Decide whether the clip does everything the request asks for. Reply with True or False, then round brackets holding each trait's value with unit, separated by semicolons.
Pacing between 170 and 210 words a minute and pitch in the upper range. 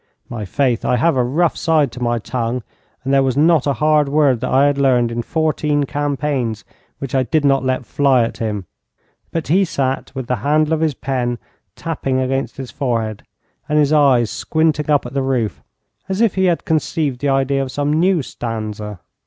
False (200 wpm; 135 Hz)